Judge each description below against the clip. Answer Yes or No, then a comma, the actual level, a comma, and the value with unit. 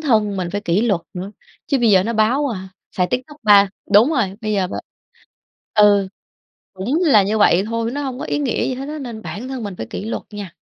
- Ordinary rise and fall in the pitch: Yes, average, 4.2 semitones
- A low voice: No, high, 215 Hz